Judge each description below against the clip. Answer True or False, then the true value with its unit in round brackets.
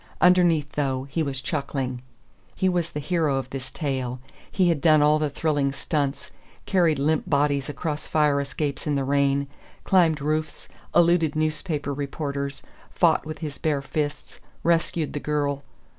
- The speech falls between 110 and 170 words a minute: True (155 wpm)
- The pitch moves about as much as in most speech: False (2.1 semitones)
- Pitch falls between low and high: True (150 Hz)